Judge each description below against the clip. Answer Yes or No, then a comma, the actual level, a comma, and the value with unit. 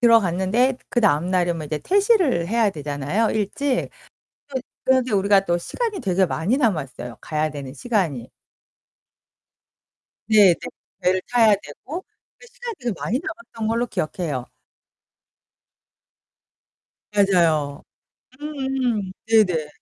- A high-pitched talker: Yes, high, 200 Hz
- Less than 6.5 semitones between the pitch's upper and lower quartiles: No, wide, 6.8 semitones